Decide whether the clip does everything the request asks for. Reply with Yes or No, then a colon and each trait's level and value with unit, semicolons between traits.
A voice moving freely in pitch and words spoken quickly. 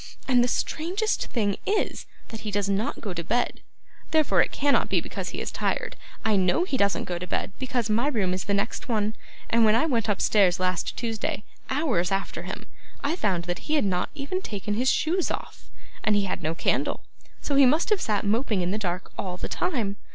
Yes: wide, 5.7 semitones; fast, 215 wpm